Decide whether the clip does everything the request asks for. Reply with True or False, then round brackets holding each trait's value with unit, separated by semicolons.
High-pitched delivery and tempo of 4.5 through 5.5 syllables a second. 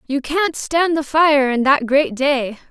False (285 Hz; 3.7 syllables/s)